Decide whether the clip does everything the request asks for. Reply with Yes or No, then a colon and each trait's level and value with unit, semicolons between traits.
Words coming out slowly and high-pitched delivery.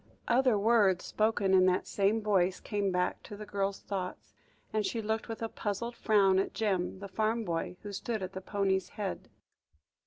No: average, 185 wpm; high, 200 Hz